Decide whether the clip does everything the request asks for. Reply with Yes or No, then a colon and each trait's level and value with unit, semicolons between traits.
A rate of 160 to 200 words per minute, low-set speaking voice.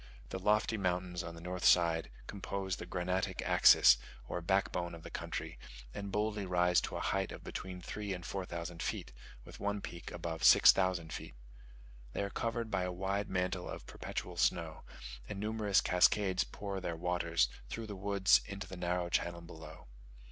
Yes: average, 175 wpm; very low, 90 Hz